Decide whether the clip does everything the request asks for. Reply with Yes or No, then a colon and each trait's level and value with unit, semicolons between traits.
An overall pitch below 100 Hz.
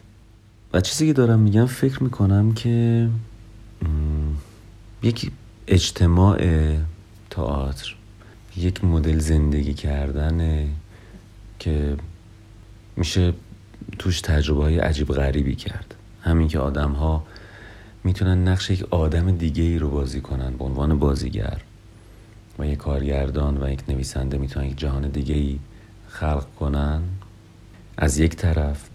Yes: very low, 90 Hz